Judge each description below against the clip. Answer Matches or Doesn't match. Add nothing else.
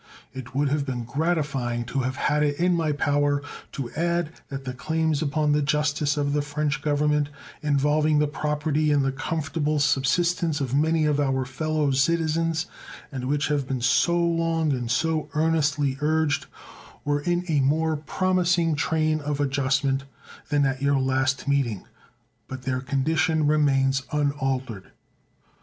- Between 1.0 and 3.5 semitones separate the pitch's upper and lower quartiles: Matches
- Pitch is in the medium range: Matches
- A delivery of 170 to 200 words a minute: Doesn't match